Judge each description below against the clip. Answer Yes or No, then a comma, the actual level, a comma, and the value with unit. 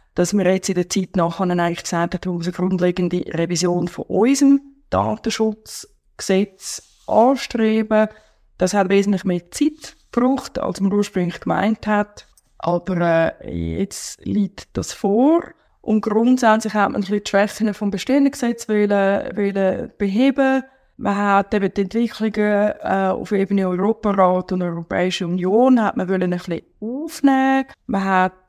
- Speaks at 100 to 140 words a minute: Yes, average, 135 wpm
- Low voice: No, high, 200 Hz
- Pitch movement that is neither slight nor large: Yes, average, 3.4 semitones